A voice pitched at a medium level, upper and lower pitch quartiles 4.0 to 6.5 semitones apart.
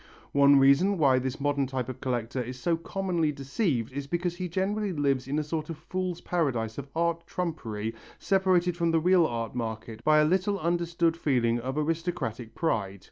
Yes: medium, 150 Hz; average, 5.1 semitones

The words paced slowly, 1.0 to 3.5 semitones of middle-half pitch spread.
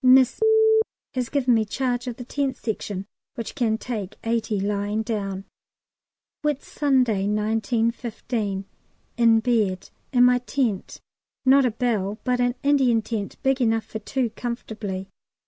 Yes: slow, 130 wpm; average, 3.1 semitones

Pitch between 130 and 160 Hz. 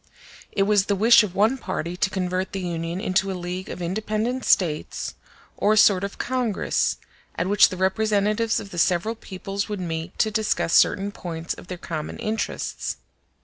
No: high, 195 Hz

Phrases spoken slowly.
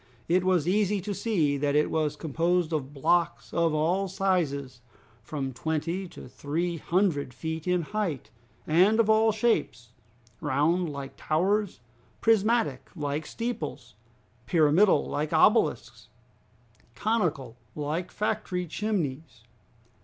Yes: slow, 115 wpm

